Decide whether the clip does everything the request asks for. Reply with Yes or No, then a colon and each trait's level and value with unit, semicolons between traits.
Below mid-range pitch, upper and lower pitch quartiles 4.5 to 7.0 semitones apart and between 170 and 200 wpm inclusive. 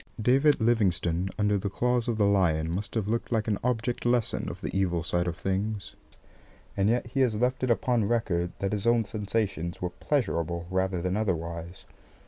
Yes: low, 100 Hz; average, 4.8 semitones; average, 185 wpm